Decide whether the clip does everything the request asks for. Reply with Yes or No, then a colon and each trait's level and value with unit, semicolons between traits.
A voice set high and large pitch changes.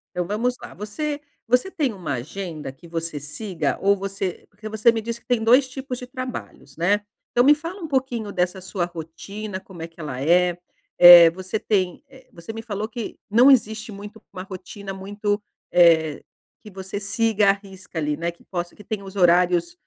No: high, 200 Hz; average, 4.3 semitones